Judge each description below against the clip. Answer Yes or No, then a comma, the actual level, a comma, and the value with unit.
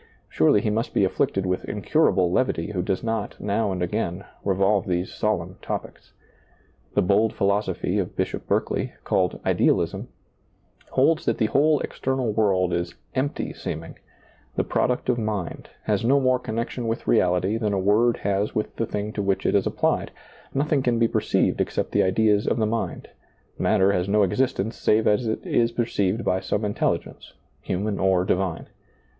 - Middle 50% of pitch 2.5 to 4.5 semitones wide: Yes, average, 3.3 semitones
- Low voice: Yes, low, 105 Hz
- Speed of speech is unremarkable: Yes, average, 170 wpm